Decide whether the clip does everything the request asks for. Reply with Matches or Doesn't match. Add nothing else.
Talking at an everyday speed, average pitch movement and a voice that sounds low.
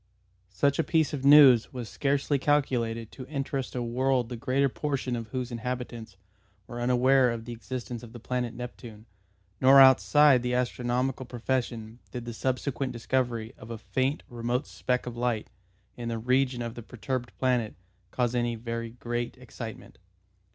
Doesn't match